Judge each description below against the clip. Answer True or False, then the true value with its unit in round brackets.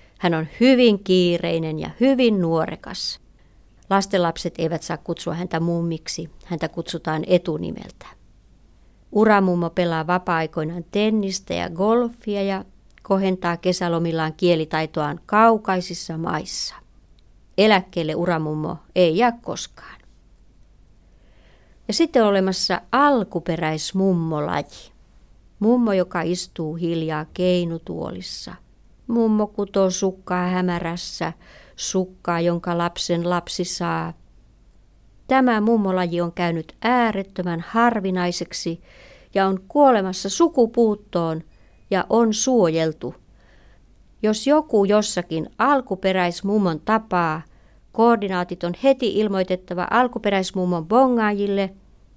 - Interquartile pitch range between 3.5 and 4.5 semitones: True (3.8 semitones)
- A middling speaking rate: False (85 wpm)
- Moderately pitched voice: True (180 Hz)